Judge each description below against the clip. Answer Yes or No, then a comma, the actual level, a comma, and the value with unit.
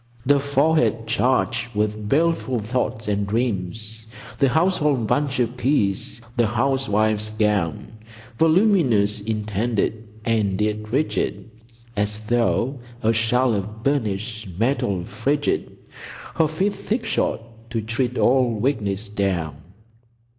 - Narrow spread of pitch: No, average, 4.1 semitones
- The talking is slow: Yes, slow, 110 wpm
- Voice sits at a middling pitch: No, low, 115 Hz